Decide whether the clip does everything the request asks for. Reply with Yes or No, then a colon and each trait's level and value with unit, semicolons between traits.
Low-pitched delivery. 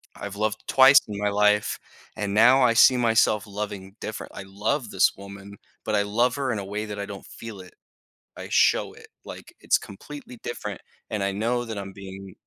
Yes: low, 105 Hz